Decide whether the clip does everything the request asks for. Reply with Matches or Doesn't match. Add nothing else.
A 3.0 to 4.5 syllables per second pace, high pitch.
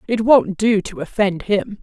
Matches